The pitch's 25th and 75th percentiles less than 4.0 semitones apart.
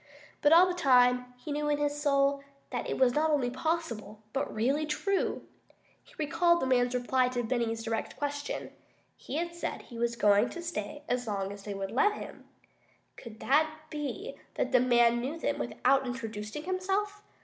No: average, 4.7 semitones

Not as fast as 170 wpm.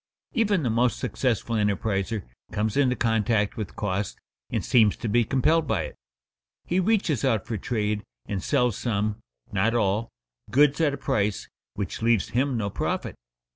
Yes: average, 160 wpm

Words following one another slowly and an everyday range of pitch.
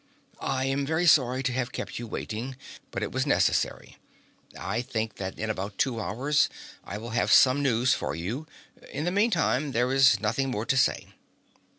No: average, 185 wpm; average, 3.6 semitones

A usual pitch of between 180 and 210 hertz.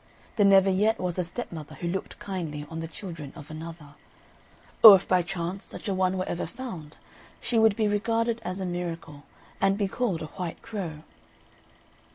Yes: medium, 185 Hz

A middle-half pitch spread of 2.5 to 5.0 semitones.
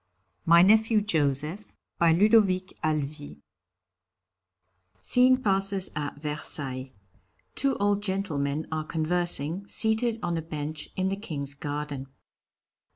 No: wide, 5.4 semitones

